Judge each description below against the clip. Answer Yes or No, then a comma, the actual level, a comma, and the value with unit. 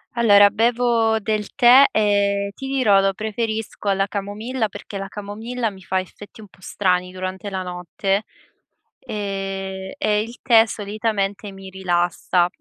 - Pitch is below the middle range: No, high, 205 Hz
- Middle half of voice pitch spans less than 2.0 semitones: No, narrow, 2.4 semitones